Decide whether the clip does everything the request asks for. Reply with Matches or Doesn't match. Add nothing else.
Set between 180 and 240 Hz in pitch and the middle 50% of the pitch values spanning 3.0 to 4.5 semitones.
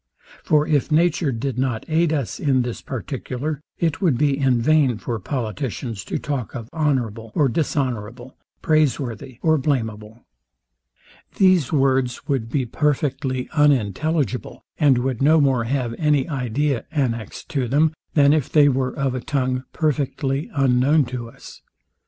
Doesn't match